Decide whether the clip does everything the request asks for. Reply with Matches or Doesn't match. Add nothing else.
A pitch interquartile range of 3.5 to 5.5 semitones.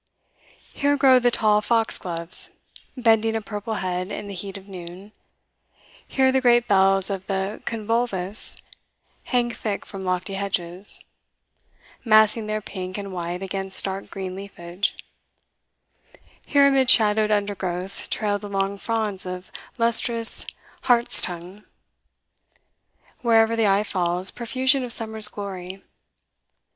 Doesn't match